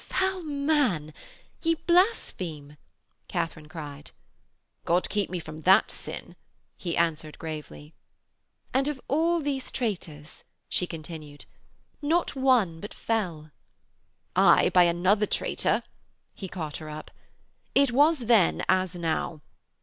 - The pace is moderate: No, slow, 120 wpm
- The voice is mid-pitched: Yes, medium, 180 Hz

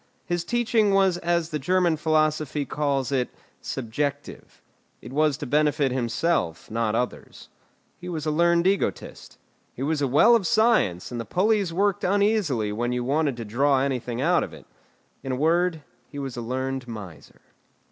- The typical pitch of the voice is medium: Yes, medium, 150 Hz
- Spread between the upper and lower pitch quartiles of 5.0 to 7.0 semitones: Yes, wide, 5.5 semitones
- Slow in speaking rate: No, average, 165 wpm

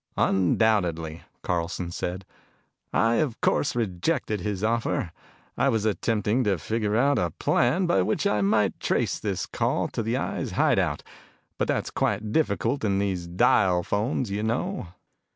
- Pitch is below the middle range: Yes, low, 105 Hz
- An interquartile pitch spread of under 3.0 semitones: No, average, 3.9 semitones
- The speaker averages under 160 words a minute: Yes, average, 150 wpm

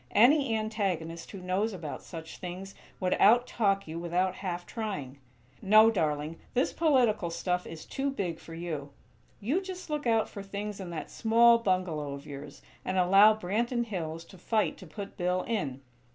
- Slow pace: No, average, 170 wpm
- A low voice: No, high, 190 Hz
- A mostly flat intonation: No, average, 4.8 semitones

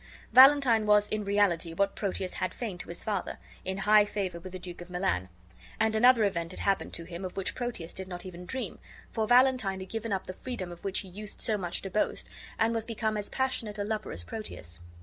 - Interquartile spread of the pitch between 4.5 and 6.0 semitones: No, average, 3.3 semitones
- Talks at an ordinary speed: No, fast, 230 wpm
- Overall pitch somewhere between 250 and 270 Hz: No, high, 200 Hz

